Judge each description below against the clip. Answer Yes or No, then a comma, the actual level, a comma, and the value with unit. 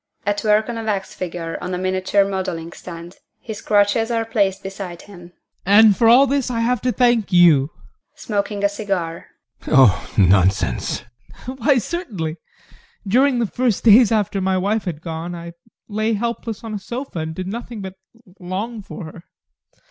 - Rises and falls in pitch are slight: No, average, 4.4 semitones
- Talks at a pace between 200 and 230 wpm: No, average, 175 wpm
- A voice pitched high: Yes, high, 200 Hz